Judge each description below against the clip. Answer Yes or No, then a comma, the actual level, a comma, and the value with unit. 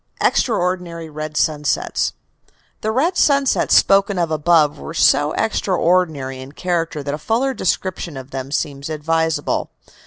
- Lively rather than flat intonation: No, average, 4.0 semitones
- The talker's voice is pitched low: No, medium, 165 Hz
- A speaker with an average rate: No, slow, 130 wpm